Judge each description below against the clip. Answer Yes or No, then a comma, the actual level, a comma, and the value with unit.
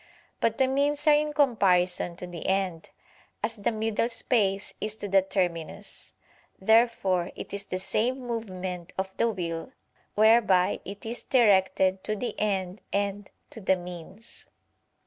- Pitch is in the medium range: No, high, 200 Hz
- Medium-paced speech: Yes, average, 145 wpm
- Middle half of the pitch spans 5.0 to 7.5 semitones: No, average, 3.7 semitones